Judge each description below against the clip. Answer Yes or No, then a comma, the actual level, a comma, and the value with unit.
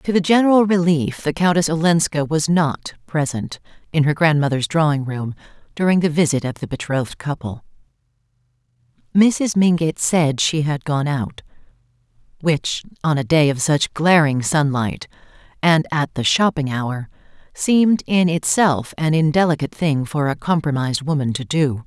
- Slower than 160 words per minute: Yes, average, 150 wpm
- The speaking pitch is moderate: Yes, medium, 155 Hz